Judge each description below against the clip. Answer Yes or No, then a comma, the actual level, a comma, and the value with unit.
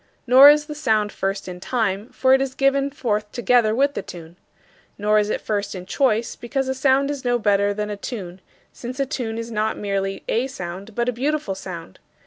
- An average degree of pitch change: Yes, average, 4.6 semitones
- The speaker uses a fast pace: Yes, fast, 210 wpm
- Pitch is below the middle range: No, high, 225 Hz